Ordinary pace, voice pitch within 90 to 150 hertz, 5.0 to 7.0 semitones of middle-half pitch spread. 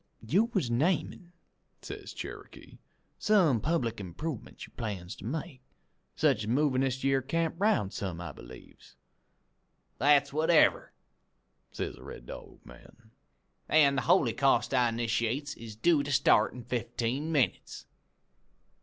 No: slow, 130 wpm; low, 135 Hz; average, 5.3 semitones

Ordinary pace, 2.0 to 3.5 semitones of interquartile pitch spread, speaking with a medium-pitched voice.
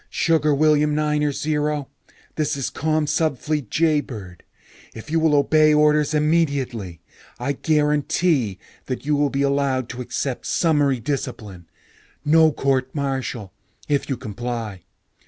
No: slow, 120 wpm; average, 3.1 semitones; medium, 145 Hz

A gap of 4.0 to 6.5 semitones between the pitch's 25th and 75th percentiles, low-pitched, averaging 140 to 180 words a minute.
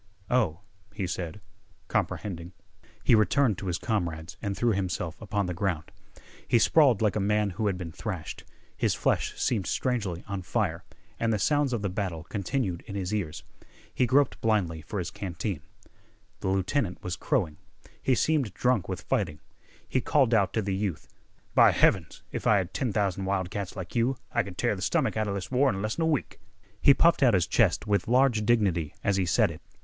No: average, 4.4 semitones; low, 100 Hz; average, 195 wpm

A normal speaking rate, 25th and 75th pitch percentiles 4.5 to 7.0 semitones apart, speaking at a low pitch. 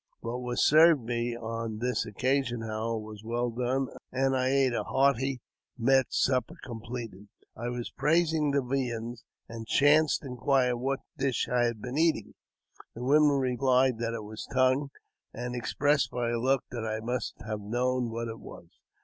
No: average, 165 wpm; narrow, 2.5 semitones; low, 125 Hz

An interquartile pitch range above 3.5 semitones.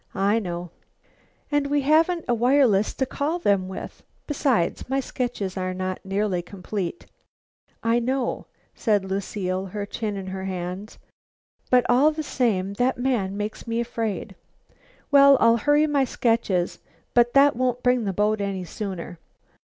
Yes: average, 5.2 semitones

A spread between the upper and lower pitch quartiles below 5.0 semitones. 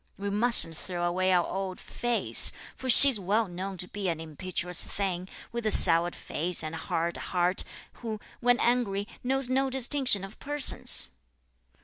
No: average, 5.3 semitones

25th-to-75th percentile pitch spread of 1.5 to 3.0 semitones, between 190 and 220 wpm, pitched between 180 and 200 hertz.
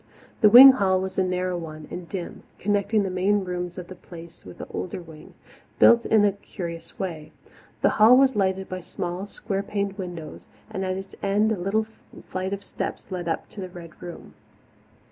Yes: narrow, 2.4 semitones; average, 195 wpm; medium, 185 Hz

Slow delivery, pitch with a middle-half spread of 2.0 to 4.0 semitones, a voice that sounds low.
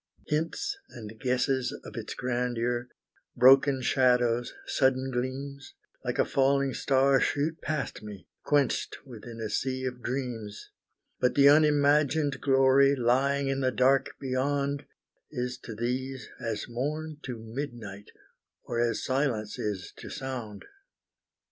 Yes: slow, 125 wpm; narrow, 2.4 semitones; low, 130 Hz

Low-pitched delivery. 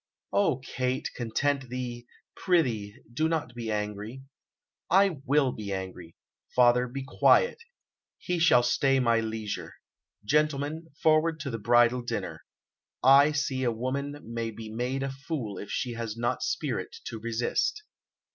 Yes: low, 125 Hz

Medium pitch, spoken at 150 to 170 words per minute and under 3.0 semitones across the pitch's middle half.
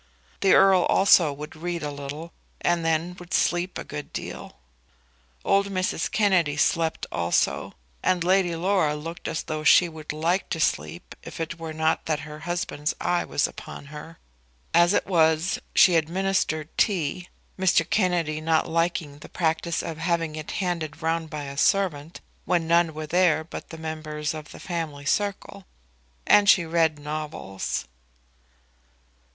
Yes: medium, 165 Hz; average, 155 wpm; narrow, 2.4 semitones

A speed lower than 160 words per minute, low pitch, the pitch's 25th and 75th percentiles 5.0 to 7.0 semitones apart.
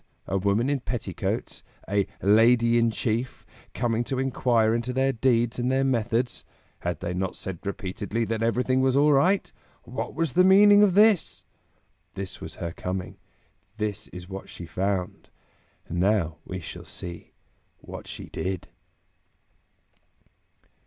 Yes: average, 140 wpm; low, 115 Hz; average, 5.3 semitones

